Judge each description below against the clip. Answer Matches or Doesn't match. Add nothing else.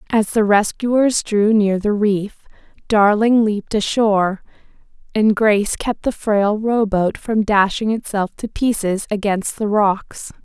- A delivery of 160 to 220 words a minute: Doesn't match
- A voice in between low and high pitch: Doesn't match